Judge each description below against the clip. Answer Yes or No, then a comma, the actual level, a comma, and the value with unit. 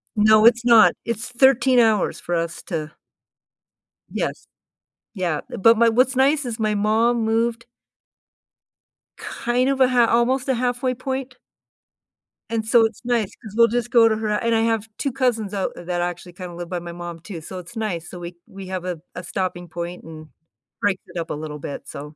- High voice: Yes, high, 220 Hz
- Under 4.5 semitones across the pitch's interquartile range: No, average, 5.2 semitones